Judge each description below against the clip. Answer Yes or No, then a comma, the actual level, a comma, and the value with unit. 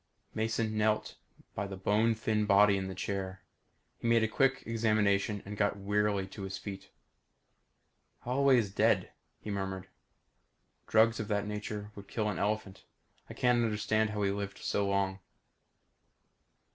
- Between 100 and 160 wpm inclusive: Yes, average, 150 wpm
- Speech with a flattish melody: Yes, narrow, 1.8 semitones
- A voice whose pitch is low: Yes, low, 105 Hz